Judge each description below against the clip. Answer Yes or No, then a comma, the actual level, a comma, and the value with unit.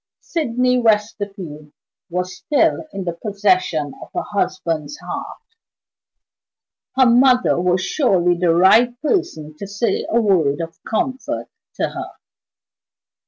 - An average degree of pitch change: No, wide, 5.9 semitones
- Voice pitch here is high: Yes, high, 200 Hz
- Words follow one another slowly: Yes, slow, 115 wpm